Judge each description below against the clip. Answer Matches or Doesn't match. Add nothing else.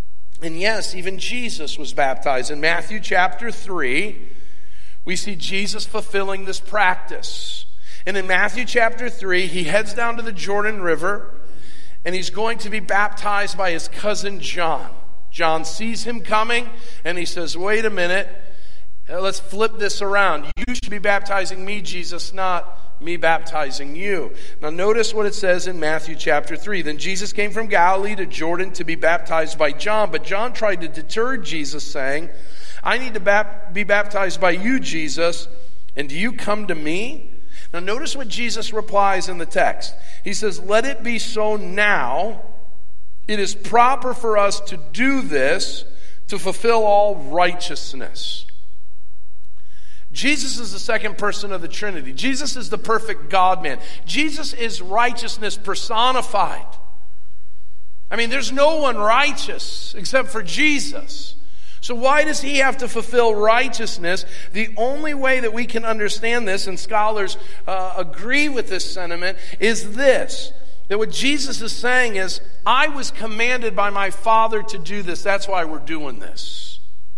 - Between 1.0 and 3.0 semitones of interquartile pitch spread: Doesn't match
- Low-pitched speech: Doesn't match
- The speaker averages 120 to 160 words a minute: Matches